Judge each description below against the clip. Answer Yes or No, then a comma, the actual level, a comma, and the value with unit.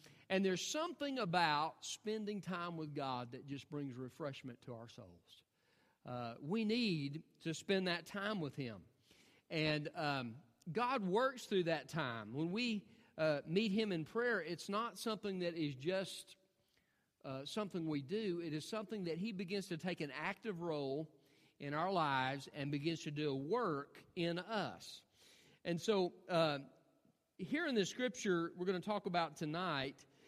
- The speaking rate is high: No, average, 165 wpm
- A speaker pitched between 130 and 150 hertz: No, medium, 170 Hz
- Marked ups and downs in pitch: Yes, wide, 5.7 semitones